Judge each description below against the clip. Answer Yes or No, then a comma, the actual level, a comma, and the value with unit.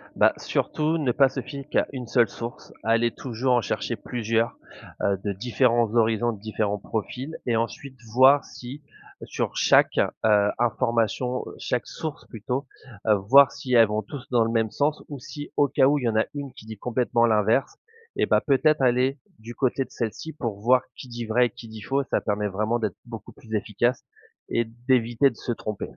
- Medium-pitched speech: No, low, 120 Hz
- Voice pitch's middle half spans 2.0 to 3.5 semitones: Yes, average, 3.0 semitones